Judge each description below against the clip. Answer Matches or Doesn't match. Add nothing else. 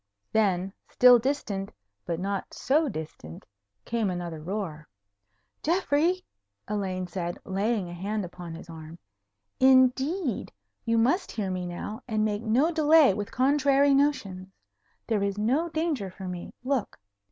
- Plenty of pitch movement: Matches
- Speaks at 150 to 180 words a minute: Doesn't match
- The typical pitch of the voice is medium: Doesn't match